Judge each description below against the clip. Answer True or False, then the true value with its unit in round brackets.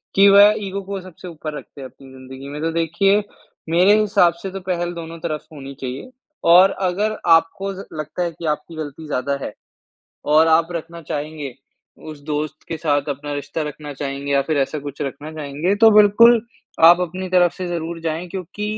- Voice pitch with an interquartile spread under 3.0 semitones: False (4.1 semitones)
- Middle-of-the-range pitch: True (165 Hz)